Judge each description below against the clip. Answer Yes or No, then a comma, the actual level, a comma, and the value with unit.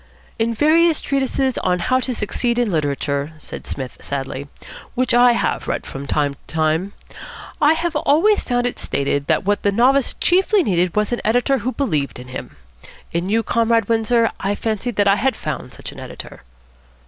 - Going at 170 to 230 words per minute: Yes, average, 185 wpm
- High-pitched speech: Yes, high, 225 Hz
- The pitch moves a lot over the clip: Yes, wide, 7.5 semitones